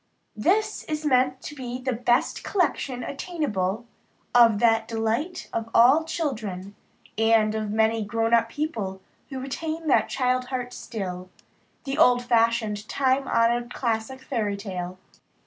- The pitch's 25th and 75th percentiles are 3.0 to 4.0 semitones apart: Yes, average, 3.5 semitones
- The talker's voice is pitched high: Yes, high, 240 Hz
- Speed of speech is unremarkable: No, slow, 130 wpm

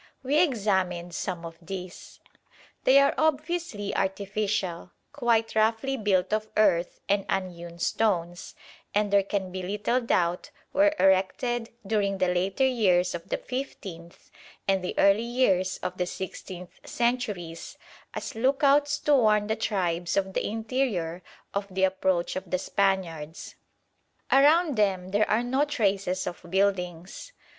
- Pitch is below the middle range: No, high, 195 Hz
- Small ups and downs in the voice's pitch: No, average, 4.4 semitones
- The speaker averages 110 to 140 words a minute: Yes, slow, 135 wpm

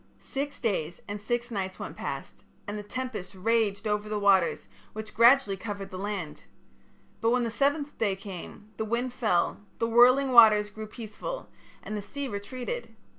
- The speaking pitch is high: Yes, high, 215 Hz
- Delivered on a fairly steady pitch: No, average, 3.3 semitones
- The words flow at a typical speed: Yes, average, 170 wpm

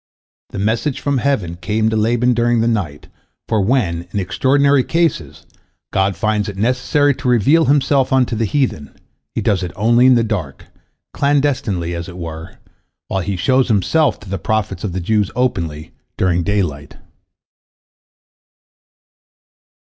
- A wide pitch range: Yes, wide, 5.8 semitones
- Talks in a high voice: No, low, 110 Hz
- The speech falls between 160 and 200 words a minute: No, average, 150 wpm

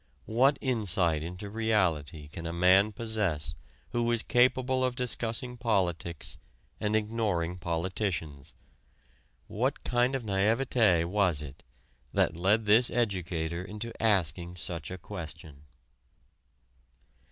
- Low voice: Yes, very low, 95 Hz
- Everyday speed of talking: No, slow, 110 wpm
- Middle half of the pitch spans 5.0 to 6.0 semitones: Yes, average, 5.3 semitones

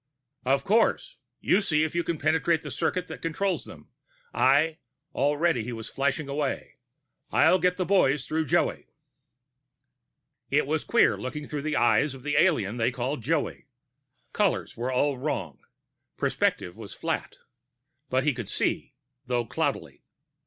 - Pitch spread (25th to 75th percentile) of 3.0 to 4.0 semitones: No, average, 4.4 semitones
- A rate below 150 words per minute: No, average, 155 wpm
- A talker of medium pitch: Yes, medium, 145 Hz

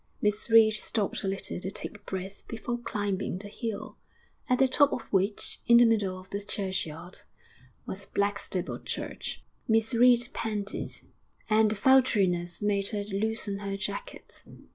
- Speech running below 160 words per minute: Yes, average, 150 wpm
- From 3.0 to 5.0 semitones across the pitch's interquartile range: No, narrow, 2.5 semitones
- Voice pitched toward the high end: Yes, high, 205 Hz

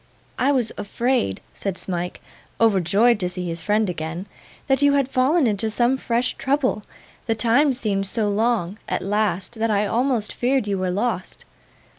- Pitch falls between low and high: No, high, 220 Hz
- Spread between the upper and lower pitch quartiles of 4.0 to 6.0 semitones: Yes, average, 4.3 semitones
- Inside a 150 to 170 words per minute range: Yes, average, 165 wpm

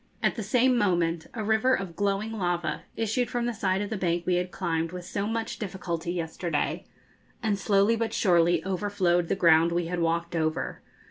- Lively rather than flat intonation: No, average, 3.9 semitones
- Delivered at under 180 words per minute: No, average, 190 wpm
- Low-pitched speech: No, medium, 185 Hz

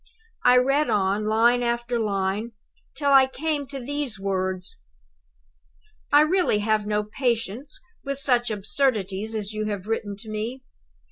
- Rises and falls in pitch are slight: No, average, 4.3 semitones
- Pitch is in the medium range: No, high, 225 Hz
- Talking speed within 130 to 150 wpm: Yes, average, 140 wpm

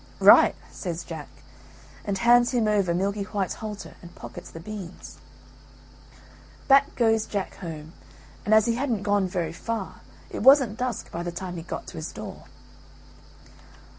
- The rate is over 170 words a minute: No, average, 155 wpm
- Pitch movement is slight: No, average, 4.4 semitones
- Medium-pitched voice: No, high, 200 Hz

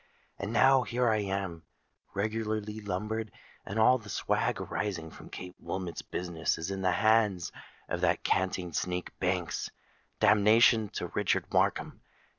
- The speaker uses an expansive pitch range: No, average, 3.3 semitones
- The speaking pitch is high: No, low, 100 Hz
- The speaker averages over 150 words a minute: No, slow, 135 wpm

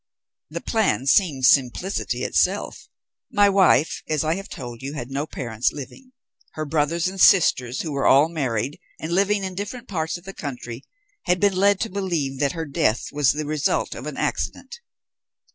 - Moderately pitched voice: Yes, medium, 155 Hz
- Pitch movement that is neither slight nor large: No, wide, 5.8 semitones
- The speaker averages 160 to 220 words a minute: Yes, average, 180 wpm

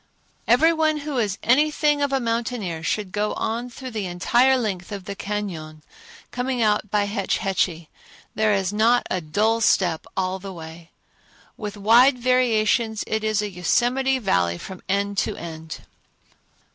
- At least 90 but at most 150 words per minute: No, average, 160 wpm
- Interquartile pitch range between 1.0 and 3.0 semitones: No, average, 4.7 semitones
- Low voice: No, high, 210 Hz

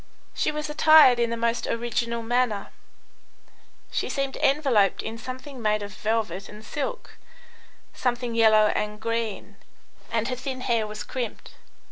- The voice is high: Yes, high, 235 Hz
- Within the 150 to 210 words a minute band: No, average, 140 wpm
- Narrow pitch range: No, average, 3.0 semitones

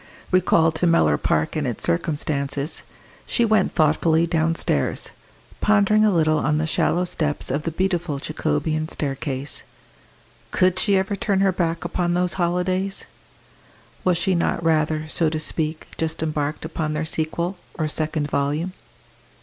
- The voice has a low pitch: No, medium, 160 Hz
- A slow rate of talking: No, average, 145 wpm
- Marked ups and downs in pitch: No, average, 2.8 semitones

